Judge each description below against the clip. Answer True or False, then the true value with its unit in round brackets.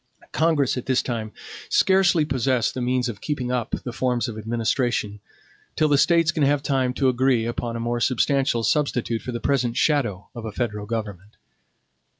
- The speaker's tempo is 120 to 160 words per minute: False (175 wpm)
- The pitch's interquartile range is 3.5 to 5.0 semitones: False (3.0 semitones)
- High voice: False (125 Hz)